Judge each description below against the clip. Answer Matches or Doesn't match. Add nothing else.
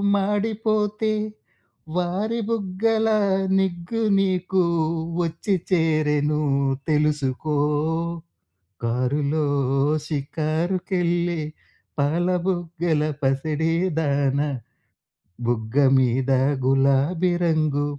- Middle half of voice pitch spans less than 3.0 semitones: Doesn't match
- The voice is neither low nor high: Matches